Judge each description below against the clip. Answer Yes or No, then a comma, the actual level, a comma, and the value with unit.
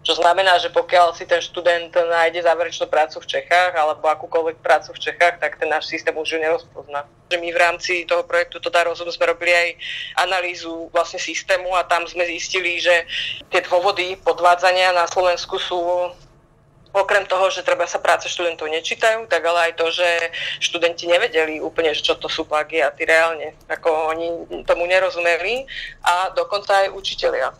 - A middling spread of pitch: No, narrow, 1.5 semitones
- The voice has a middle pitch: Yes, medium, 170 Hz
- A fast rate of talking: Yes, fast, 175 wpm